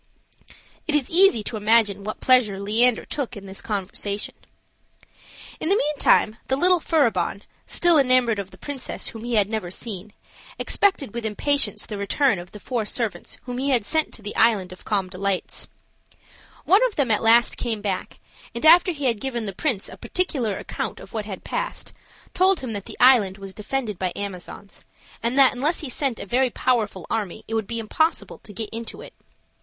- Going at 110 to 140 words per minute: No, average, 190 wpm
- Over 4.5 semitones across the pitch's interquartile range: Yes, average, 4.9 semitones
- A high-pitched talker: Yes, high, 225 Hz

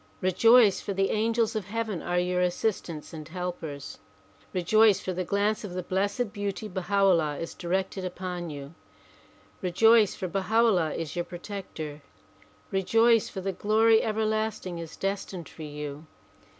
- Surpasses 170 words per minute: No, average, 150 wpm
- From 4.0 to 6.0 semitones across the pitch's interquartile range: No, average, 3.6 semitones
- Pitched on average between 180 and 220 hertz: Yes, high, 190 Hz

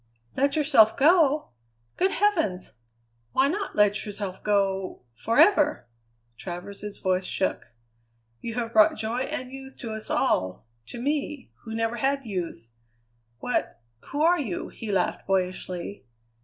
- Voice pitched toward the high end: Yes, high, 225 Hz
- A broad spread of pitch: Yes, wide, 6.5 semitones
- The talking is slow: Yes, slow, 130 wpm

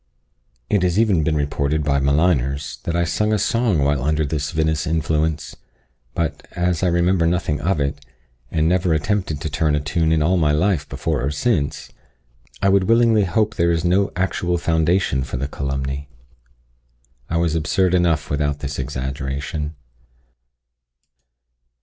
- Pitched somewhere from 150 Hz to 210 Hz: No, very low, 80 Hz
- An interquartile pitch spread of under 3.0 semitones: No, average, 3.6 semitones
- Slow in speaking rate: No, average, 155 wpm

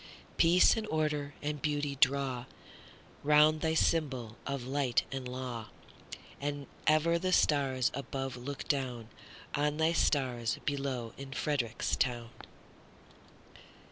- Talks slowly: Yes, slow, 105 wpm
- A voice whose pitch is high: No, medium, 140 Hz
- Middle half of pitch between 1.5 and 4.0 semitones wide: Yes, average, 2.8 semitones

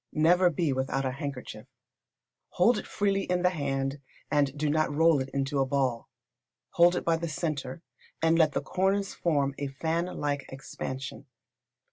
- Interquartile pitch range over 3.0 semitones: Yes, average, 3.9 semitones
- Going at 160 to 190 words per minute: Yes, average, 165 wpm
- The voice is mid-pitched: Yes, medium, 150 Hz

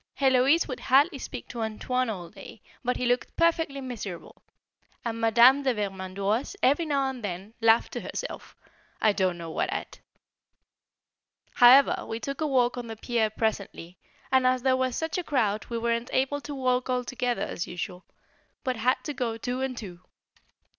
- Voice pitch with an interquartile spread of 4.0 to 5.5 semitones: No, average, 3.3 semitones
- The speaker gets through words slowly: No, average, 175 wpm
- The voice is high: Yes, high, 245 Hz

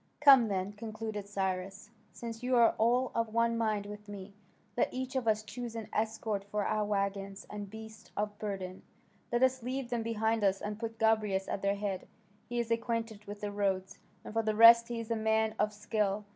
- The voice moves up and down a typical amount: No, narrow, 2.1 semitones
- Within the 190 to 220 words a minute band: Yes, average, 200 wpm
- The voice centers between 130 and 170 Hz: No, high, 215 Hz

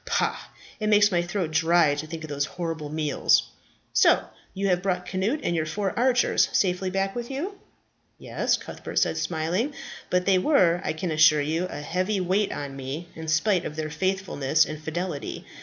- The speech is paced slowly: No, average, 185 wpm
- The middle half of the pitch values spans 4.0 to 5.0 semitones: No, average, 3.6 semitones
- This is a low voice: No, medium, 175 Hz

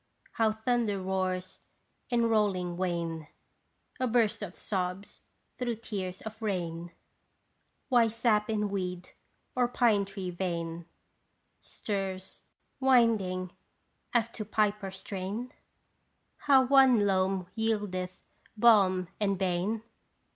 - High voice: Yes, high, 200 Hz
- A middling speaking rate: No, slow, 105 wpm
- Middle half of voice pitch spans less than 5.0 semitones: Yes, average, 3.5 semitones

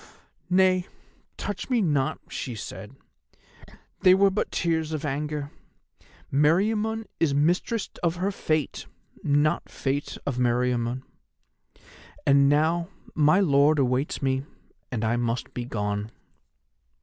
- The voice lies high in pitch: No, medium, 145 Hz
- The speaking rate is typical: No, slow, 115 wpm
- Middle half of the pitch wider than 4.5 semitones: Yes, average, 5.2 semitones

